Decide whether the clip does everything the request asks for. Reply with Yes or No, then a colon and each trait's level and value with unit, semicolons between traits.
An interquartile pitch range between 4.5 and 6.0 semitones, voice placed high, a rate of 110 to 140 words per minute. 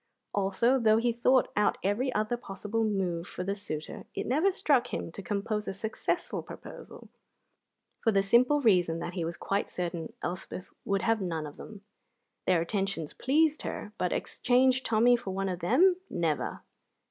No: average, 4.9 semitones; high, 205 Hz; average, 170 wpm